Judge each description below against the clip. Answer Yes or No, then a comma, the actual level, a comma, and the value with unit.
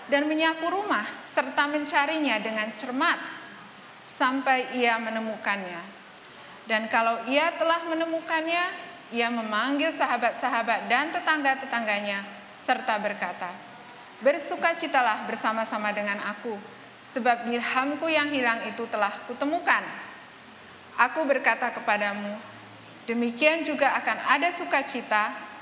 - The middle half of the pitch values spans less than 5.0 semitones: No, wide, 5.5 semitones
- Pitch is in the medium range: No, high, 245 Hz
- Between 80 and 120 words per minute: Yes, average, 95 wpm